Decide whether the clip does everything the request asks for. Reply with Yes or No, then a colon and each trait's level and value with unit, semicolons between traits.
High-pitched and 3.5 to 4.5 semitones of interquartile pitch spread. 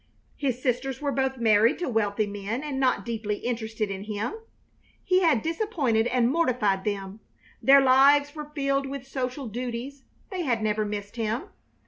Yes: very high, 250 Hz; average, 4.2 semitones